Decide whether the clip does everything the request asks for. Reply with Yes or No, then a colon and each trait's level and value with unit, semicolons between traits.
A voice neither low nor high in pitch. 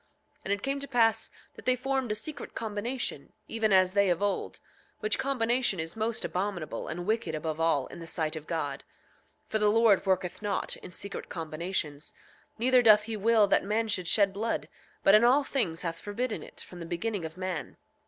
No: high, 205 Hz